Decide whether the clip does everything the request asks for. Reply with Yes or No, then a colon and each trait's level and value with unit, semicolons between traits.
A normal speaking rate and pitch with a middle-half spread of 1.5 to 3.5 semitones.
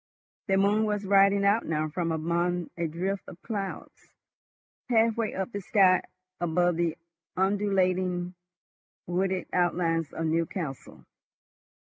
No: slow, 115 wpm; average, 2.8 semitones